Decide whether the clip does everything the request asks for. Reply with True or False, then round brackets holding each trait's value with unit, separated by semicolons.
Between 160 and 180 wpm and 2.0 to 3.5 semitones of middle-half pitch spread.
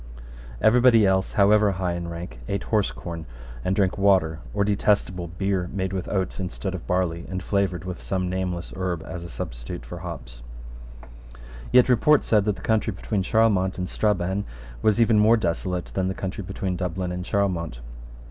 True (175 wpm; 2.4 semitones)